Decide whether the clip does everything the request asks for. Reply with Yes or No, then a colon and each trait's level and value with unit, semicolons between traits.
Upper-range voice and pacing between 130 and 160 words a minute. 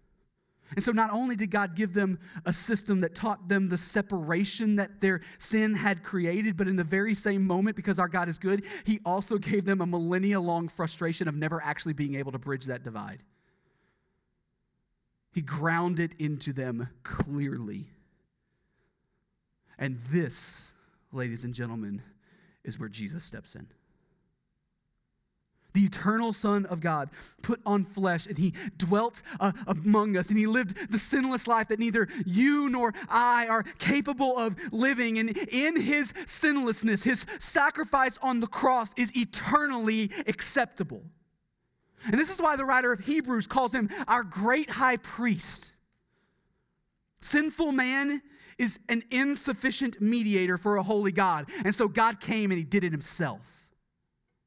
Yes: high, 200 Hz; average, 150 wpm